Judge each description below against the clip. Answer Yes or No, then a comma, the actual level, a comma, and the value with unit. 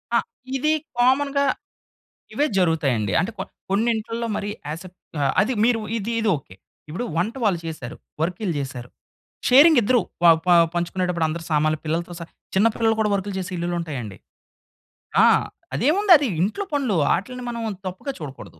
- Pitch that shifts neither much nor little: No, wide, 6.5 semitones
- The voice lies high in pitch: Yes, high, 195 Hz